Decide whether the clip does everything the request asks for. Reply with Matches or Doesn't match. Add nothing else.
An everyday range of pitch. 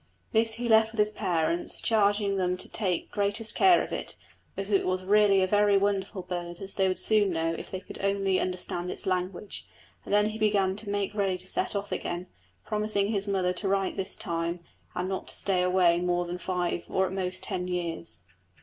Doesn't match